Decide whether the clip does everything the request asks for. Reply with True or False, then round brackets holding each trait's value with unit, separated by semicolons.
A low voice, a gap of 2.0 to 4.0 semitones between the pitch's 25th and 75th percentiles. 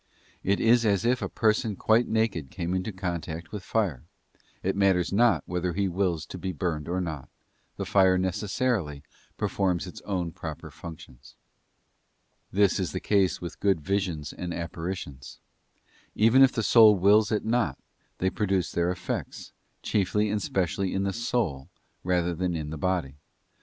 True (95 Hz; 3.4 semitones)